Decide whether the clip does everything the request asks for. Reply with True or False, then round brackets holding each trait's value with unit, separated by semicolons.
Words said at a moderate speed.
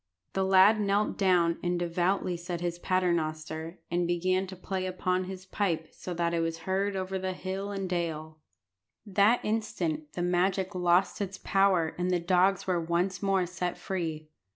True (165 wpm)